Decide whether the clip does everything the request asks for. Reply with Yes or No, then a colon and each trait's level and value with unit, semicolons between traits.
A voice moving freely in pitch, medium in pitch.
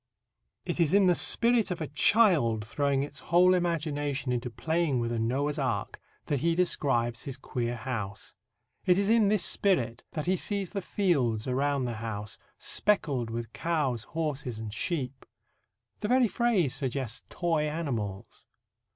Yes: wide, 6.7 semitones; medium, 145 Hz